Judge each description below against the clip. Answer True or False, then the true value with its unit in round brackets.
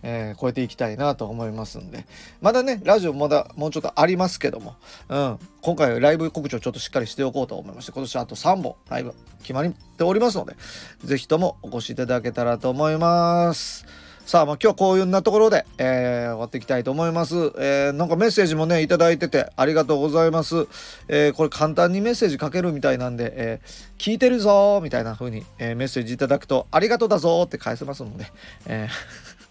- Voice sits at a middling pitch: True (150 Hz)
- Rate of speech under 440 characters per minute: False (465 characters per minute)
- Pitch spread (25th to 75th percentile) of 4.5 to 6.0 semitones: True (5.6 semitones)